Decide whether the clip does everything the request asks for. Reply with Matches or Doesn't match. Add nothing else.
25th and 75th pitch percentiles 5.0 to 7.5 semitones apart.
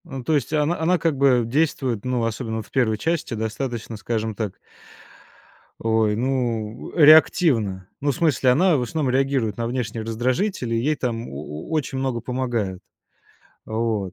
Doesn't match